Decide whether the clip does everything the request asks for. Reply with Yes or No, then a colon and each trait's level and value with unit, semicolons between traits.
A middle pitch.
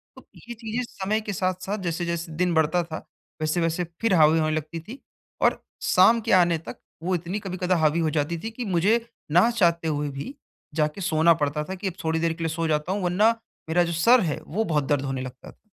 Yes: medium, 170 Hz